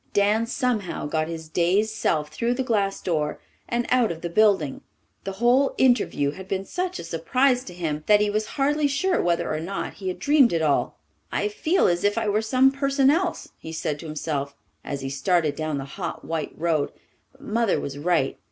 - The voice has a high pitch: Yes, high, 195 Hz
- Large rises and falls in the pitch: Yes, wide, 7.6 semitones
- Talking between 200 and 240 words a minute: Yes, fast, 205 wpm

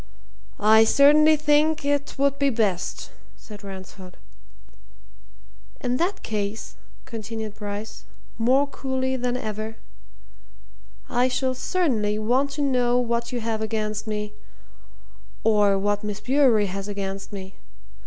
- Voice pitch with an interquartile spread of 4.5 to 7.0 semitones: No, average, 4.1 semitones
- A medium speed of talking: No, slow, 120 wpm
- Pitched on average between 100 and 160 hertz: No, high, 225 Hz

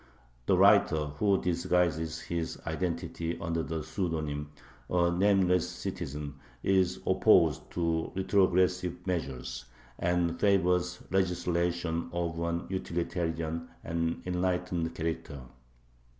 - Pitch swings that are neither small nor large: No, narrow, 1.8 semitones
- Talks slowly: Yes, slow, 95 wpm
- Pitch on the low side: Yes, very low, 85 Hz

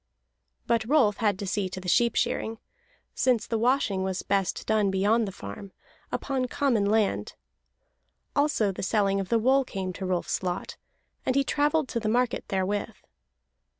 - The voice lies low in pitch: No, high, 215 Hz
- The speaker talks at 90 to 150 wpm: No, average, 165 wpm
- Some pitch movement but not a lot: Yes, average, 4.3 semitones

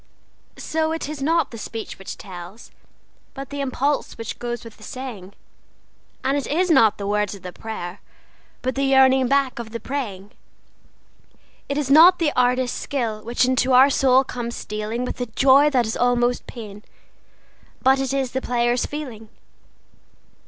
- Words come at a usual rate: Yes, average, 165 wpm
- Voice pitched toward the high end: Yes, very high, 250 Hz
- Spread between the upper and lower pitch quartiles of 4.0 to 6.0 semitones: No, average, 3.6 semitones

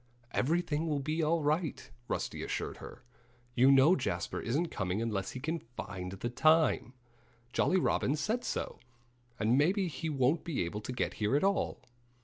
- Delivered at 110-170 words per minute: Yes, average, 165 wpm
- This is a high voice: No, medium, 145 Hz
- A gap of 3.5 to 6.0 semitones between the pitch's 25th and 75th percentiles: Yes, wide, 5.4 semitones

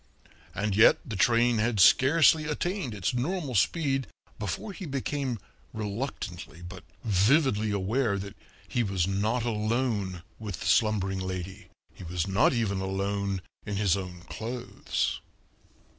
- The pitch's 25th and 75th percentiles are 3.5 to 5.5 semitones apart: Yes, average, 4.4 semitones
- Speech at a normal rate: No, slow, 130 wpm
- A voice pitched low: Yes, low, 105 Hz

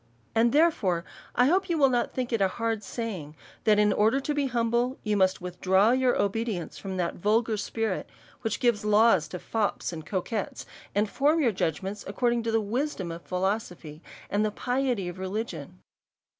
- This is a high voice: Yes, high, 215 Hz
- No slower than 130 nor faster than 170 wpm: No, average, 180 wpm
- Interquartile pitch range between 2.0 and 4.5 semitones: Yes, average, 4.1 semitones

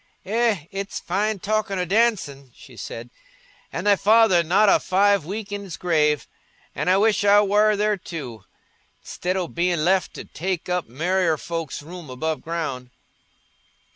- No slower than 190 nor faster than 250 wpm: No, average, 155 wpm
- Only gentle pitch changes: No, average, 4.3 semitones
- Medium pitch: Yes, medium, 180 Hz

